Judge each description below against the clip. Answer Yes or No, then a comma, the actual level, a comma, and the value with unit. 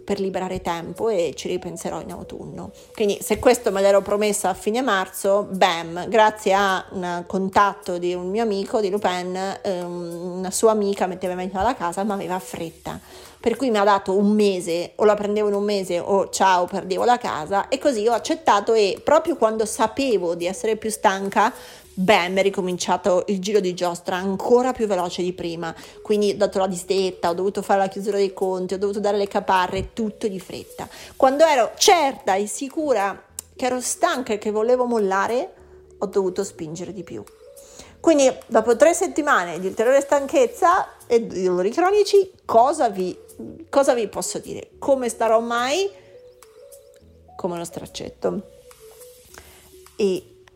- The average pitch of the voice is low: No, high, 205 Hz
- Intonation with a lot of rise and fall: No, average, 4.7 semitones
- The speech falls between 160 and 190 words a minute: Yes, fast, 170 wpm